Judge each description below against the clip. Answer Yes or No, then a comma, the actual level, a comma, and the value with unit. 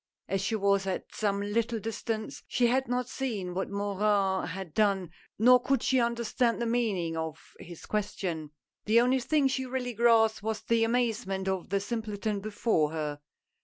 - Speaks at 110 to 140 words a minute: No, average, 165 wpm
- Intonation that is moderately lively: Yes, average, 3.6 semitones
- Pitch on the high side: Yes, high, 215 Hz